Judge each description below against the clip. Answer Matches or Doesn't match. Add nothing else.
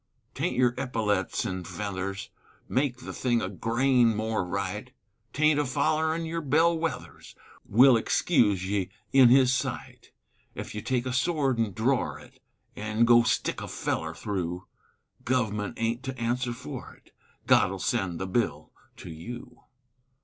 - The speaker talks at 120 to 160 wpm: Matches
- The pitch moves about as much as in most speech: Matches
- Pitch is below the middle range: Matches